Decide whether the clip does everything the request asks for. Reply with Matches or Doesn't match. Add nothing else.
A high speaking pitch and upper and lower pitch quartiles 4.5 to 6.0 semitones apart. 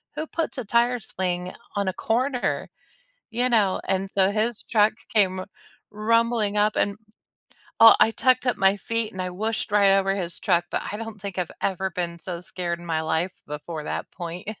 Doesn't match